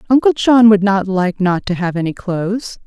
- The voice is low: No, high, 200 Hz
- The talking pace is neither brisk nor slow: No, fast, 210 wpm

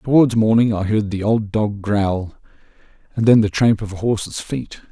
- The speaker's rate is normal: Yes, average, 195 wpm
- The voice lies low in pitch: Yes, low, 105 Hz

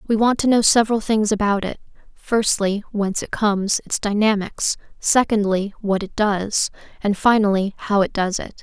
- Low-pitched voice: No, high, 210 Hz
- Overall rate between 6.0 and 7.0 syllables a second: No, 5.0 syllables/s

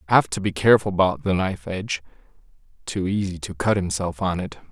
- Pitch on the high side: No, very low, 95 Hz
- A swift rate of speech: No, average, 190 wpm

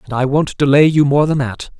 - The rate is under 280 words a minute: Yes, fast, 270 wpm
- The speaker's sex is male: Yes, male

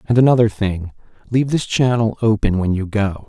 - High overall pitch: No, low, 110 Hz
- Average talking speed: Yes, average, 185 wpm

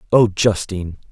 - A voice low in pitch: Yes, low, 100 Hz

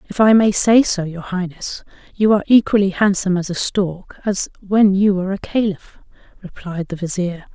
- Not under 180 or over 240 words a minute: Yes, average, 185 wpm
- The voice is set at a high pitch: Yes, high, 195 Hz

